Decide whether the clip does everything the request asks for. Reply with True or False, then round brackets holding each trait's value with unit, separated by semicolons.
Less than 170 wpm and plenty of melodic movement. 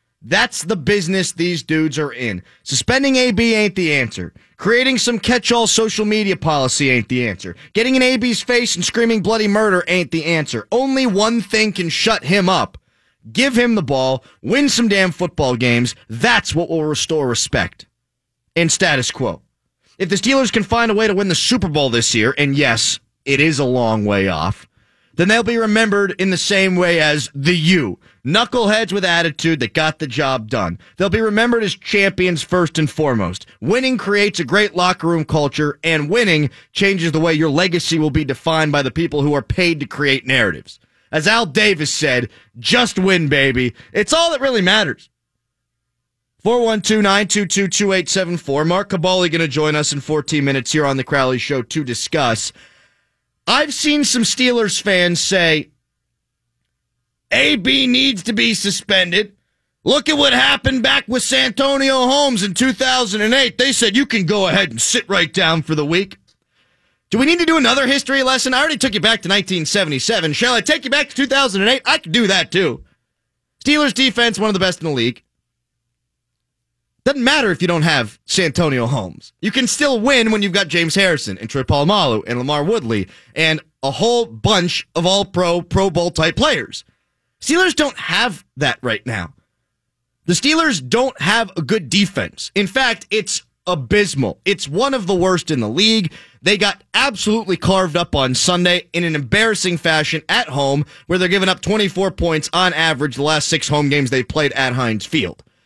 False (180 wpm; 7.5 semitones)